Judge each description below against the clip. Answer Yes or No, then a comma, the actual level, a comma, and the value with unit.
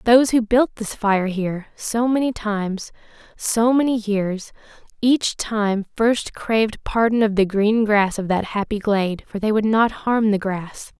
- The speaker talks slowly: No, average, 175 wpm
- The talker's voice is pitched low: No, high, 215 Hz